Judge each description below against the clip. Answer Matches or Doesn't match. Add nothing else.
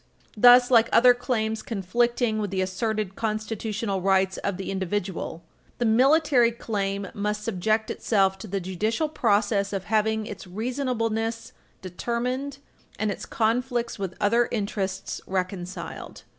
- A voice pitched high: Matches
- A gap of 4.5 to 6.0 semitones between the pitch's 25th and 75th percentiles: Doesn't match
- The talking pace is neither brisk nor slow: Doesn't match